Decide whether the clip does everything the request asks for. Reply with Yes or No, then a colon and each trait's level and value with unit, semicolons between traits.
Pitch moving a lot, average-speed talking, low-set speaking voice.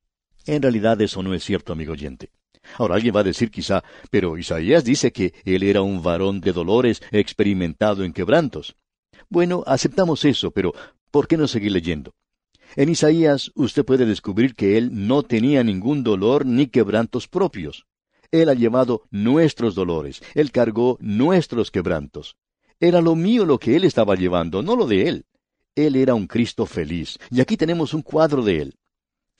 Yes: wide, 7.0 semitones; average, 170 wpm; low, 115 Hz